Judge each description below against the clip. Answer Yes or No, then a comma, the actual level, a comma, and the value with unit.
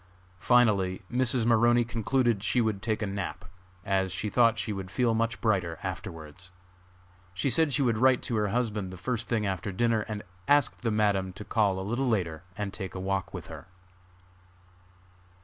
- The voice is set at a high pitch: No, low, 110 Hz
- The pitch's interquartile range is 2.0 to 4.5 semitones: Yes, average, 3.7 semitones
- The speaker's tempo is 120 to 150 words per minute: No, average, 180 wpm